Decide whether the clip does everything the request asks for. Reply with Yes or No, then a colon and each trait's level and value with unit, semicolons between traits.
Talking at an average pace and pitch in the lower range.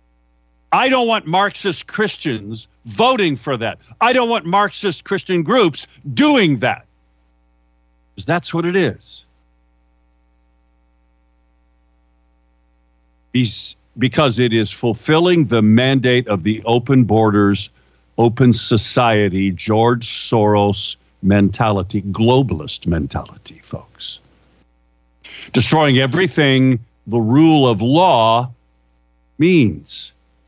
No: slow, 90 wpm; low, 110 Hz